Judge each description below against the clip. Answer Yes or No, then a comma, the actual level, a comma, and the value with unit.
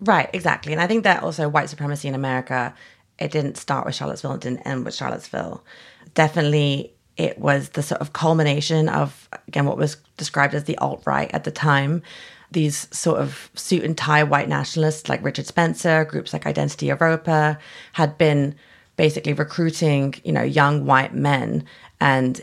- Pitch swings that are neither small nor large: No, narrow, 2.2 semitones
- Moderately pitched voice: Yes, medium, 150 Hz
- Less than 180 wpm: Yes, average, 170 wpm